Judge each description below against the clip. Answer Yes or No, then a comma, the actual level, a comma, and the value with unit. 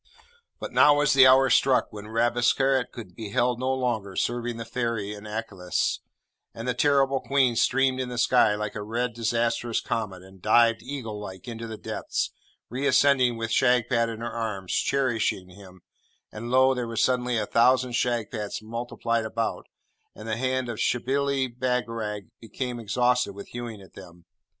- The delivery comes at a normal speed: Yes, average, 170 wpm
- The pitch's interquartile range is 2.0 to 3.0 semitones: Yes, average, 2.7 semitones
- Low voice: Yes, low, 120 Hz